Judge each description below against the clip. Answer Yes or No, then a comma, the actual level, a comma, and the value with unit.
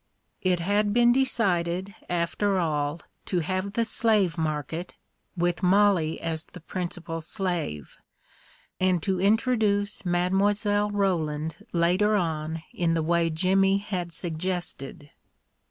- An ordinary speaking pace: No, slow, 120 wpm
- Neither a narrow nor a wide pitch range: Yes, average, 3.5 semitones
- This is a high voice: No, medium, 180 Hz